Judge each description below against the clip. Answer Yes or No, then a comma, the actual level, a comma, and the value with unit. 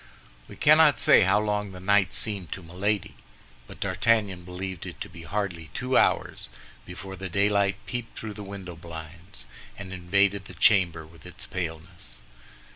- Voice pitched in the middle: No, very low, 95 Hz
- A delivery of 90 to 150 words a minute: No, average, 160 wpm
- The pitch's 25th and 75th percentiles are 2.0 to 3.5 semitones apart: Yes, average, 2.8 semitones